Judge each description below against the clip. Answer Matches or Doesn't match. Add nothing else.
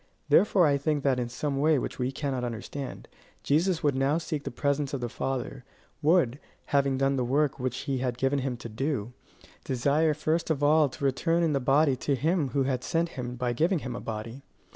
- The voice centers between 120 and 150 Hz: Matches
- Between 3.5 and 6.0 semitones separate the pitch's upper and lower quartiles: Doesn't match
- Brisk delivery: Matches